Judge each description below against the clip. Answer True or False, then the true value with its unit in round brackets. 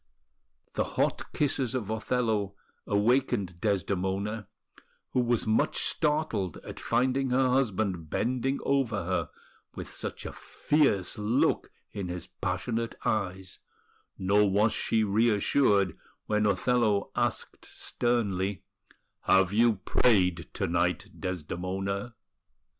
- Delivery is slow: True (110 wpm)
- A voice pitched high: False (105 Hz)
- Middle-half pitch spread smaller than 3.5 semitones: False (4.2 semitones)